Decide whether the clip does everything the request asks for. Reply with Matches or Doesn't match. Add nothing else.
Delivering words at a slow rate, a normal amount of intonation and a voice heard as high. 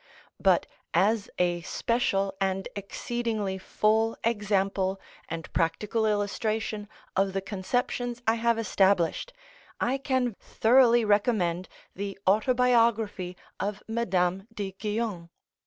Matches